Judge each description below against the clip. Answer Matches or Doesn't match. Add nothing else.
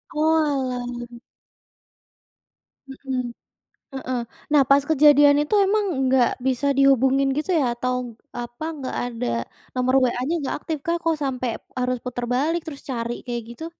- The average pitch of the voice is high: Matches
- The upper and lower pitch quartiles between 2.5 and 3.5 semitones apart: Matches